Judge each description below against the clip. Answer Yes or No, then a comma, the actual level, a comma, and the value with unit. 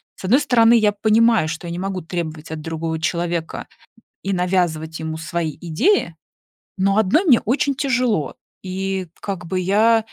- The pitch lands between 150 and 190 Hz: Yes, medium, 185 Hz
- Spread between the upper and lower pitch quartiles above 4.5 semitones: Yes, average, 5.2 semitones